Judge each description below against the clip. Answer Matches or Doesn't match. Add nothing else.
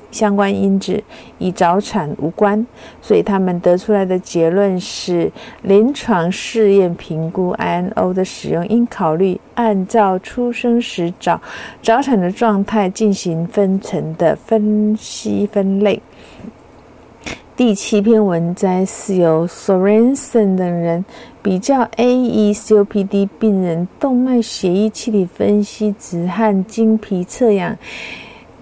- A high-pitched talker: Matches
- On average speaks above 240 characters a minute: Doesn't match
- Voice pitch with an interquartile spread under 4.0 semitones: Matches